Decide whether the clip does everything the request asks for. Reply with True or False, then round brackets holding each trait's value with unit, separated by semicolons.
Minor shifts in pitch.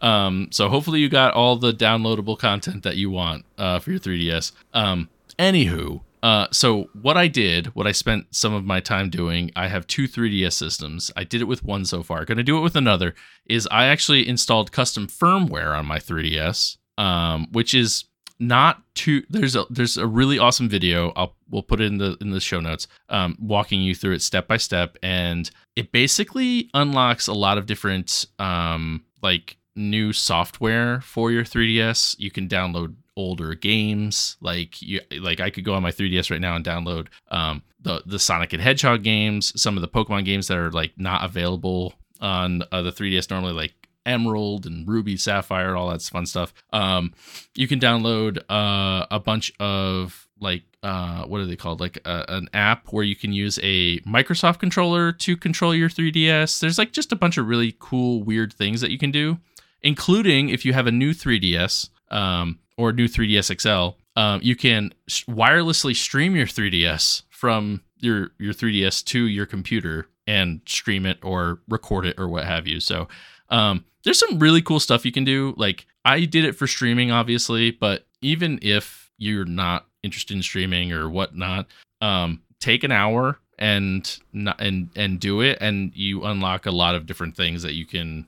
False (4.8 semitones)